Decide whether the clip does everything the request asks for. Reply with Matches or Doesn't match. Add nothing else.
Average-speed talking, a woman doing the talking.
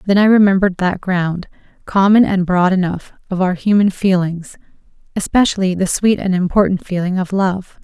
Matches